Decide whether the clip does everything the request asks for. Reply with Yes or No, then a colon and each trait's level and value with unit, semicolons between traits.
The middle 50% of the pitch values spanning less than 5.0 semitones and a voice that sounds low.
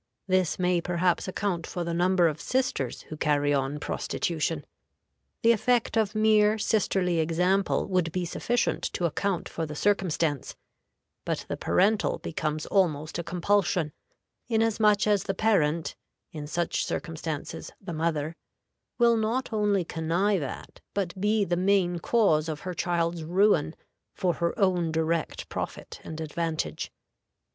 No: average, 3.9 semitones; medium, 175 Hz